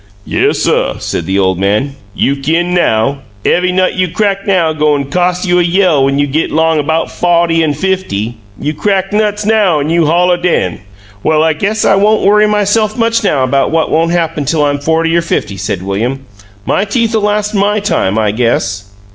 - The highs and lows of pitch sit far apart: Yes, wide, 5.8 semitones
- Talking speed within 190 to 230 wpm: Yes, average, 195 wpm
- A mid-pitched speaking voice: Yes, medium, 165 Hz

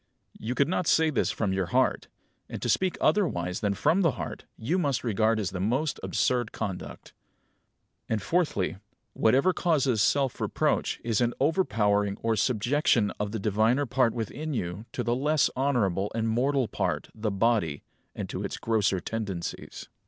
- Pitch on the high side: No, low, 115 Hz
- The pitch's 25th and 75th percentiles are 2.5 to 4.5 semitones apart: No, average, 5.3 semitones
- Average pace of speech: Yes, average, 165 wpm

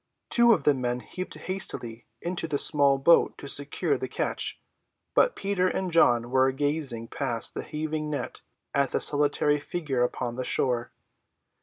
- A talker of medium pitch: Yes, medium, 145 Hz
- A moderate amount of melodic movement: Yes, average, 4.5 semitones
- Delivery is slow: No, average, 160 wpm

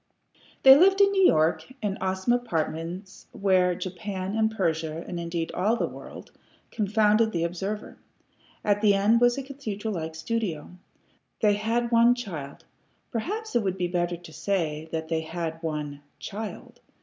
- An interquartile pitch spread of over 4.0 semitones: Yes, average, 5.1 semitones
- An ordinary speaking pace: Yes, average, 155 wpm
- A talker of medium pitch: No, high, 195 Hz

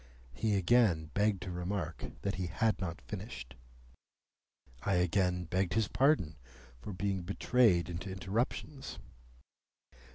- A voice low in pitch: Yes, very low, 95 Hz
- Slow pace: Yes, slow, 120 wpm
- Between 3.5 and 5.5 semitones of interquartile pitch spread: No, average, 3.1 semitones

